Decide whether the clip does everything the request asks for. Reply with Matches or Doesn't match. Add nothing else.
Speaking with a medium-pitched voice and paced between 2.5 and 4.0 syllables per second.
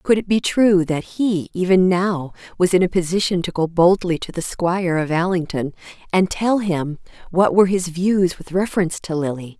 Doesn't match